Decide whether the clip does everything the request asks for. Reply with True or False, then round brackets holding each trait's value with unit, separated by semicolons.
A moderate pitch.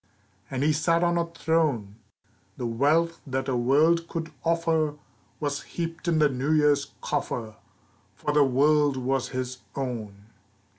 True (145 Hz)